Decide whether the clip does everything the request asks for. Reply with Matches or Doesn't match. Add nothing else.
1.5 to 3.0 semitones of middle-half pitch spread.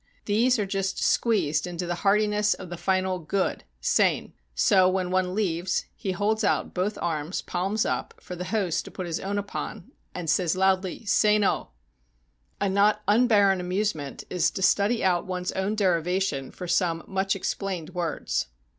Matches